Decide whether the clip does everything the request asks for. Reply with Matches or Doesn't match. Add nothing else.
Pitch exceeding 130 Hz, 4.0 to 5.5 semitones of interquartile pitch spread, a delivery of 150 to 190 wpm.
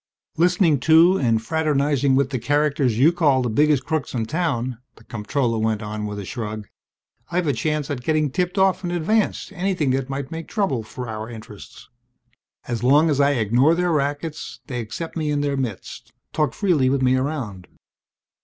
Matches